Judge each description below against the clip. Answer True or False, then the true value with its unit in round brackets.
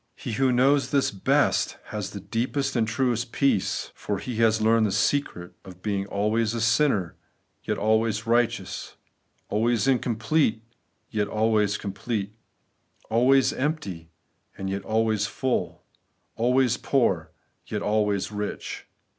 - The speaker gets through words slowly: True (130 wpm)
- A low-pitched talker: True (110 Hz)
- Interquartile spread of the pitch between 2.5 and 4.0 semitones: True (3.1 semitones)